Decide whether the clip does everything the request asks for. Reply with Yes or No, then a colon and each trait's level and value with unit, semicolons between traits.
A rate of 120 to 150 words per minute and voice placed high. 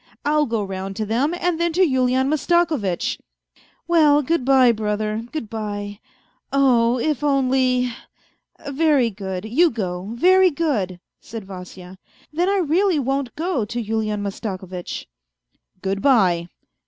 Yes: average, 140 wpm; high, 245 Hz